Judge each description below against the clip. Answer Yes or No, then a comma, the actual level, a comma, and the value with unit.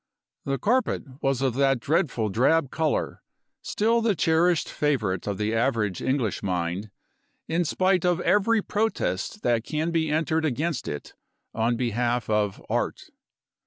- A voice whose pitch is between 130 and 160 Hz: Yes, low, 135 Hz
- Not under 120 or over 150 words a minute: Yes, average, 140 wpm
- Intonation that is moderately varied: No, wide, 6.9 semitones